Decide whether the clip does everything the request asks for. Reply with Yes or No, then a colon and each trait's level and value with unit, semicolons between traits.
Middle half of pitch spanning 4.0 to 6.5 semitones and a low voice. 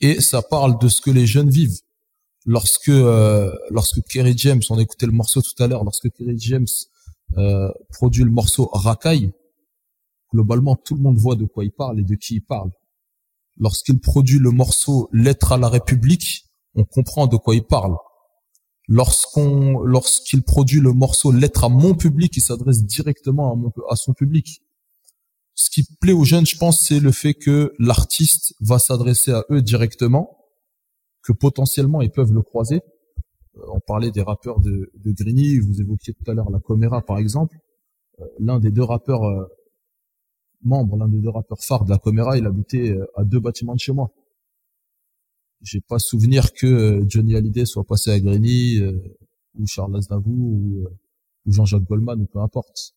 Yes: average, 4.4 semitones; low, 120 Hz